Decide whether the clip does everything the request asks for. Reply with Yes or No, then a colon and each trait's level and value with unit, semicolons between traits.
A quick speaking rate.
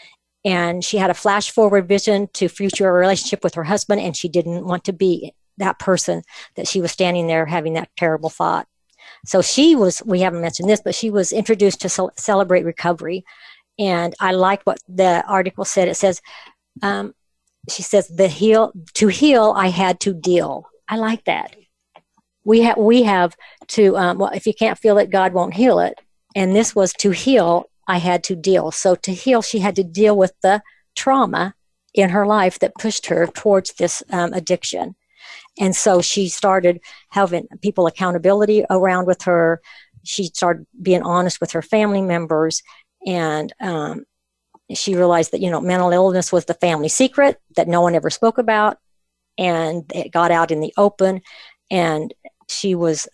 No: average, 180 wpm